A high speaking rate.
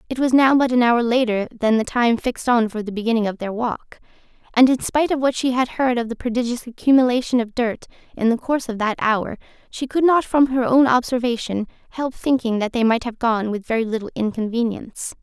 Yes: fast, 220 wpm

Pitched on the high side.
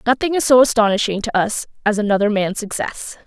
Yes: high, 220 Hz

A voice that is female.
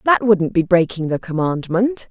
Yes: female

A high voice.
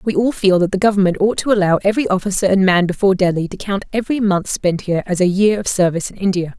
Yes: high, 195 Hz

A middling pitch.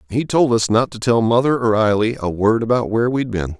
No: low, 115 Hz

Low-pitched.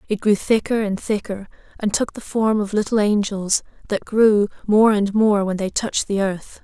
No: high, 205 Hz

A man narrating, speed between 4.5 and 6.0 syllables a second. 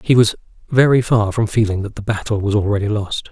Yes: male; 5.8 syllables/s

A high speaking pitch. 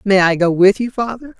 Yes: high, 205 Hz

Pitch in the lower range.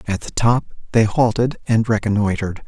Yes: low, 110 Hz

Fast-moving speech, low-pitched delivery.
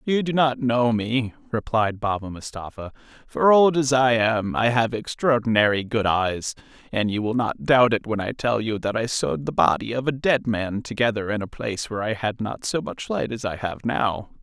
Yes: fast, 215 wpm; low, 115 Hz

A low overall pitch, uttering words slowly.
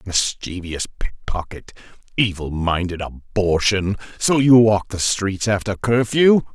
Yes: low, 100 Hz; slow, 120 wpm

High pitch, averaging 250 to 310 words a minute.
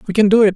No: high, 205 Hz; fast, 435 wpm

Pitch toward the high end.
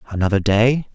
No: low, 110 Hz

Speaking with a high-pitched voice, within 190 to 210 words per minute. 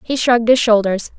Yes: high, 230 Hz; average, 200 wpm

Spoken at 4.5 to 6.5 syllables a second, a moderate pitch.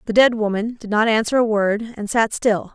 No: 5.4 syllables/s; high, 220 Hz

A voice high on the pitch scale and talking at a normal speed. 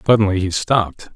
No: low, 100 Hz; average, 155 wpm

